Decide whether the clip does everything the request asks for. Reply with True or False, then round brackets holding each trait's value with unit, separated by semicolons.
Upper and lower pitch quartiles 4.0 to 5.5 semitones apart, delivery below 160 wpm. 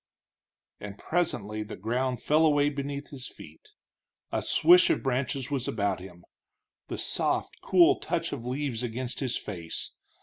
True (4.8 semitones; 145 wpm)